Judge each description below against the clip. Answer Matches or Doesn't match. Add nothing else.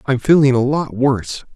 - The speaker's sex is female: Doesn't match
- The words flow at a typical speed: Matches